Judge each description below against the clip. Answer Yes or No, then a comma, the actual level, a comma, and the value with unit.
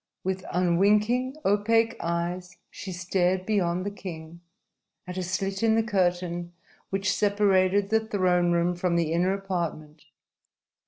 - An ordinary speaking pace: No, slow, 130 wpm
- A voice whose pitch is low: No, medium, 185 Hz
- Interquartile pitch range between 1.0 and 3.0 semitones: Yes, narrow, 2.6 semitones